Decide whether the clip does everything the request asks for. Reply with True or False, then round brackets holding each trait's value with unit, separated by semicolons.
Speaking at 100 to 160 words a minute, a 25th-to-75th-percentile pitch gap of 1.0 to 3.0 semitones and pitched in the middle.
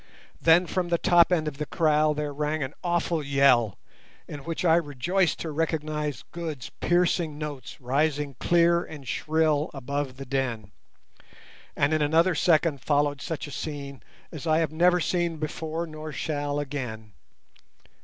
True (155 wpm; 2.7 semitones; 150 Hz)